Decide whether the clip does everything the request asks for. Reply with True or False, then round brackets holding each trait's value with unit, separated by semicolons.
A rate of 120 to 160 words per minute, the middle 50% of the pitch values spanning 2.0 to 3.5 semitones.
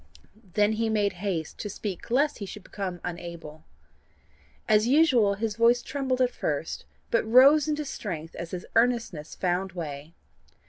False (150 wpm; 5.5 semitones)